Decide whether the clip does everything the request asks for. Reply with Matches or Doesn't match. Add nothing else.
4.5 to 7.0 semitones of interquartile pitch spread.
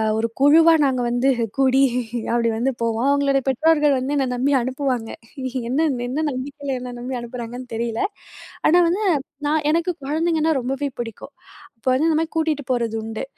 Doesn't match